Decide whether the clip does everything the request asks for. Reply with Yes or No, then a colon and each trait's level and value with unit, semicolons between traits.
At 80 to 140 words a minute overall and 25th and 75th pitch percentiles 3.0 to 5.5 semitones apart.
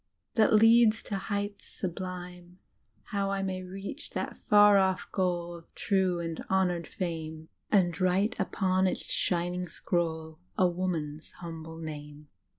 No: slow, 135 wpm; narrow, 2.6 semitones